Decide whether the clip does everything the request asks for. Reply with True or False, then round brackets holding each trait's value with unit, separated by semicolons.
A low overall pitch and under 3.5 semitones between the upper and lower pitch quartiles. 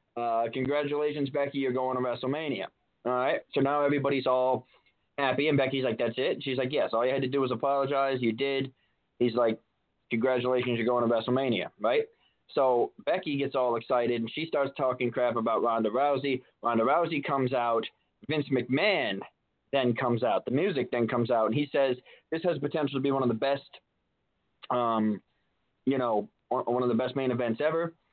True (130 Hz; 2.6 semitones)